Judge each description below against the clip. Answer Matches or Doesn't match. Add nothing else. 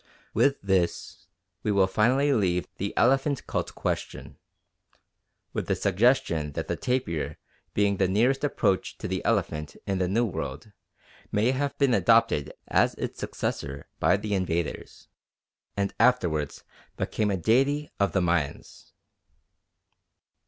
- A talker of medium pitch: Doesn't match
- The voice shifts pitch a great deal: Matches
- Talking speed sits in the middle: Doesn't match